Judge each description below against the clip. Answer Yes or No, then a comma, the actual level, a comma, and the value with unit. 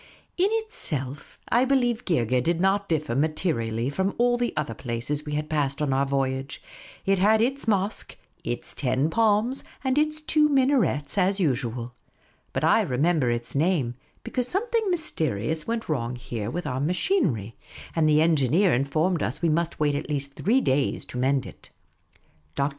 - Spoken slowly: No, average, 170 wpm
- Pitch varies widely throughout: Yes, wide, 8.4 semitones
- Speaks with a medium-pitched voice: Yes, medium, 155 Hz